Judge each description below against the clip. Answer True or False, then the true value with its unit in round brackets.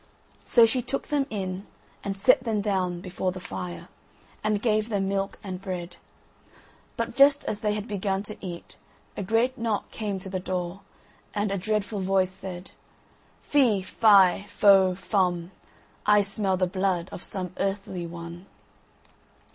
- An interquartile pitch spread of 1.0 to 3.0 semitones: True (2.5 semitones)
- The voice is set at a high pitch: True (195 Hz)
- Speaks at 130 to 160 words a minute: True (155 wpm)